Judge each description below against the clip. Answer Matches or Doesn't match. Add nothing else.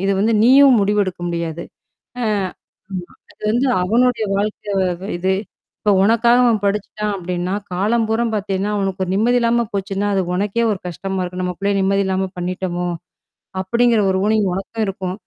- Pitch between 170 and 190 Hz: Doesn't match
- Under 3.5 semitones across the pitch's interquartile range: Matches